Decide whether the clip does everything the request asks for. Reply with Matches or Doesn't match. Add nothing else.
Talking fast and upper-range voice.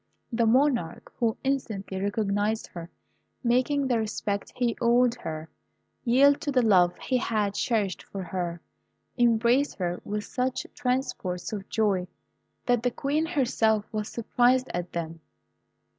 Doesn't match